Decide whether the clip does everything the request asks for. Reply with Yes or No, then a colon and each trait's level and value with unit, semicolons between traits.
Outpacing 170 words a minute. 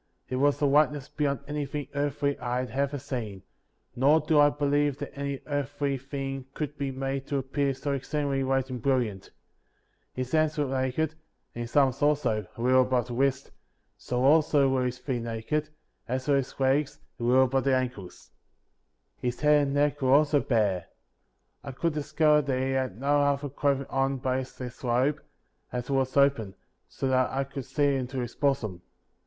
Yes: average, 185 wpm